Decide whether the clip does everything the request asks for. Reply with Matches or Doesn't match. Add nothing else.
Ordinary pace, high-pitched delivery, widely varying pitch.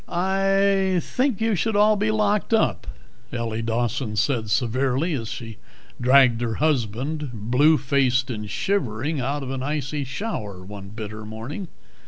Doesn't match